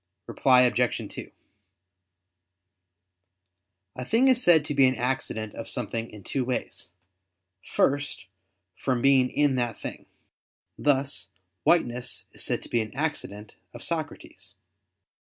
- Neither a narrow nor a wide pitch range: Yes, average, 3.4 semitones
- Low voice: Yes, low, 130 Hz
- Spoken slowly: Yes, slow, 125 wpm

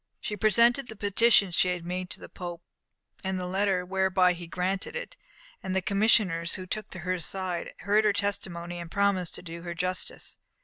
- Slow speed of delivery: No, average, 180 wpm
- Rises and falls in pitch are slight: Yes, narrow, 2.3 semitones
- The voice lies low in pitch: No, medium, 185 Hz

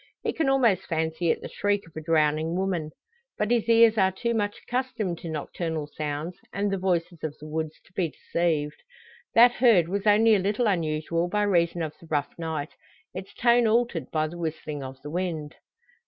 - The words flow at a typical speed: Yes, average, 195 wpm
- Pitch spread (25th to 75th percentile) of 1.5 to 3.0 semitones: No, average, 4.7 semitones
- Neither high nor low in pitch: Yes, medium, 175 Hz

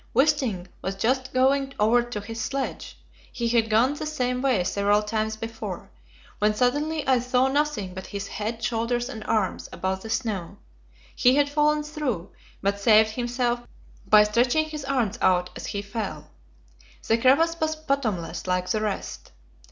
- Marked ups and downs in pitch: No, average, 4.3 semitones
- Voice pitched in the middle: No, high, 235 Hz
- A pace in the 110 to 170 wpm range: Yes, average, 160 wpm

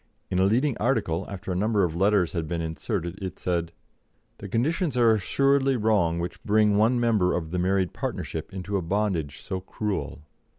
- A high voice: No, low, 100 Hz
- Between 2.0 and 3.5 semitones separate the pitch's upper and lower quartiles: No, average, 4.0 semitones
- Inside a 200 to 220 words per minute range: No, average, 180 wpm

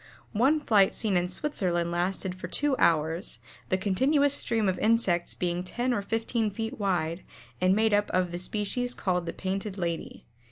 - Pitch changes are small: No, average, 4.1 semitones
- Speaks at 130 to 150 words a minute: No, average, 170 wpm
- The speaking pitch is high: Yes, high, 195 Hz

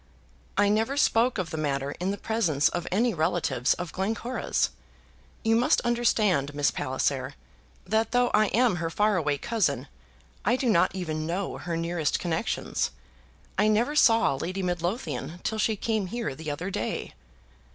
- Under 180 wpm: Yes, average, 160 wpm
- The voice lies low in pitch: No, medium, 185 Hz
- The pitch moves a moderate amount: No, wide, 5.8 semitones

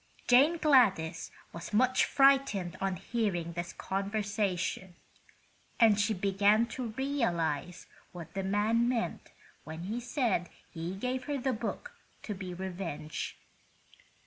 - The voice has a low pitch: No, high, 205 Hz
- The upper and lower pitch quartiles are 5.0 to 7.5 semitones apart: Yes, wide, 5.4 semitones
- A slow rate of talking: Yes, slow, 120 wpm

